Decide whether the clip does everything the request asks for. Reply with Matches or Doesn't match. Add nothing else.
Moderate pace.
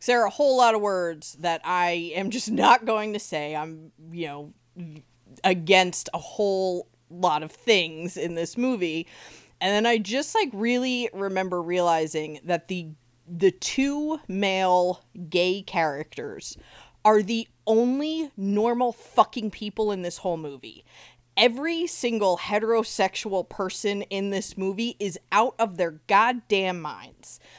Matches